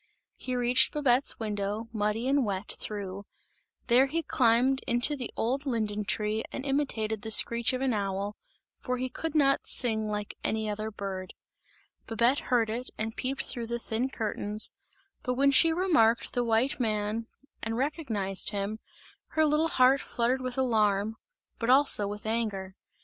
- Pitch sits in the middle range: No, high, 230 Hz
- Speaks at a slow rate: No, average, 160 wpm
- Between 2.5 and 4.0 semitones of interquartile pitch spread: Yes, average, 3.6 semitones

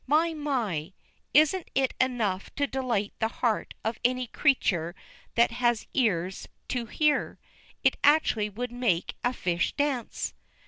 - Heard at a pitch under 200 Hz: No, high, 245 Hz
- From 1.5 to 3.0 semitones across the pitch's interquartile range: No, average, 4.6 semitones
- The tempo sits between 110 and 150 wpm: Yes, slow, 135 wpm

